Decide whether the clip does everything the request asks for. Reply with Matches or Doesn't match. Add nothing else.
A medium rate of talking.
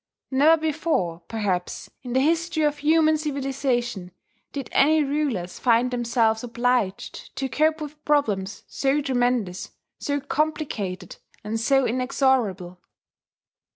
Doesn't match